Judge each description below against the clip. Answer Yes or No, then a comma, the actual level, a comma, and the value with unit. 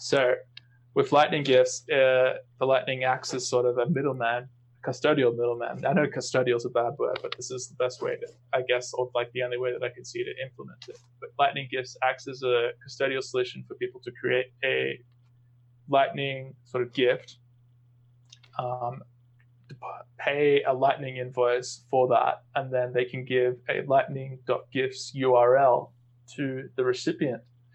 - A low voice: Yes, low, 125 Hz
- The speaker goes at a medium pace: Yes, average, 170 wpm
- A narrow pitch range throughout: Yes, narrow, 1.6 semitones